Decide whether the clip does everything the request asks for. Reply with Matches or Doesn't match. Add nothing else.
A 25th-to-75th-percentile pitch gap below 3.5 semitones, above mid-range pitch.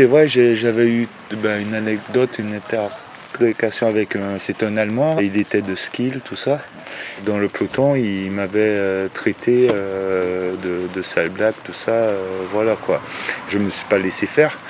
Doesn't match